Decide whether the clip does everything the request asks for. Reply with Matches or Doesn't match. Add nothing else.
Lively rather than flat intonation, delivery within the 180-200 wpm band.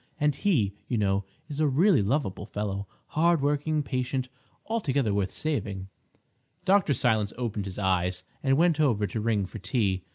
Doesn't match